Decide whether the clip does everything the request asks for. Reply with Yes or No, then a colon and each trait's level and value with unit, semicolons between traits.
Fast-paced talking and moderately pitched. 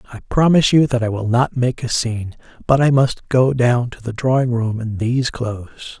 No: fast, 220 wpm; low, 120 Hz